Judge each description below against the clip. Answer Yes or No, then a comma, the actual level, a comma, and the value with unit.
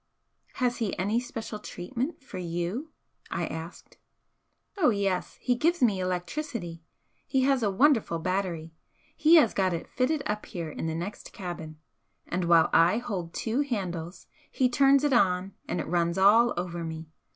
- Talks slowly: No, average, 160 wpm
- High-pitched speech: Yes, high, 195 Hz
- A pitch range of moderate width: No, wide, 6.2 semitones